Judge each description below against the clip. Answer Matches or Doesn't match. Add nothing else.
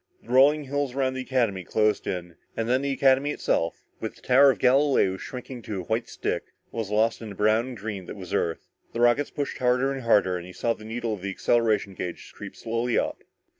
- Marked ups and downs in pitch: Doesn't match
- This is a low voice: Matches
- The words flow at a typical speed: Doesn't match